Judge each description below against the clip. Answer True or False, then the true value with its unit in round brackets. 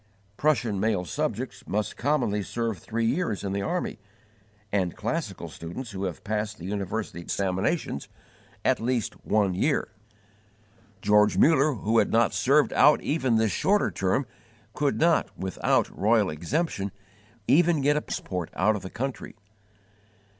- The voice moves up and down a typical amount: False (5.9 semitones)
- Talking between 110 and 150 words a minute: True (140 wpm)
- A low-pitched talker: True (110 Hz)